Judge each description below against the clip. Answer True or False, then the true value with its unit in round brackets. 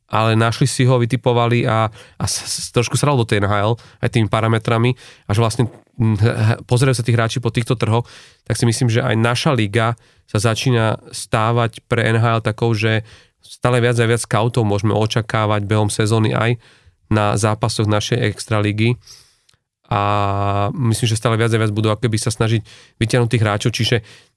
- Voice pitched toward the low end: True (115 Hz)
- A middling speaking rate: False (170 wpm)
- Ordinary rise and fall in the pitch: False (2.0 semitones)